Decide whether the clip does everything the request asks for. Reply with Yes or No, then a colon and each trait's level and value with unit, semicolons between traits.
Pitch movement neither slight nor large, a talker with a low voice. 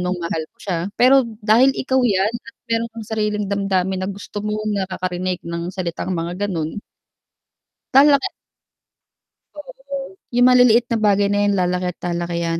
No: average, 4.7 semitones; high, 205 Hz